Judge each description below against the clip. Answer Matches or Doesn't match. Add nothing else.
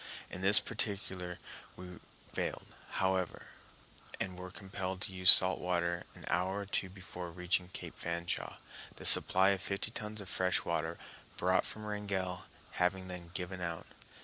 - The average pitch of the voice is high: Doesn't match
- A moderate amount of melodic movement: Doesn't match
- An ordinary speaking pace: Matches